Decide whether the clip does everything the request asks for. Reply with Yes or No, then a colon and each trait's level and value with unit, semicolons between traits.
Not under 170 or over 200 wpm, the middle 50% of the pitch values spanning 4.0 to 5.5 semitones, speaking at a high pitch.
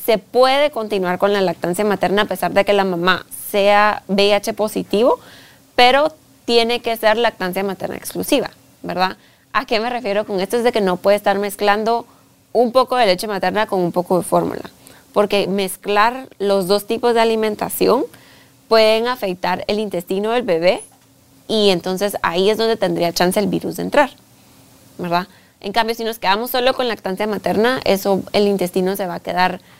No: average, 175 wpm; average, 3.1 semitones; high, 205 Hz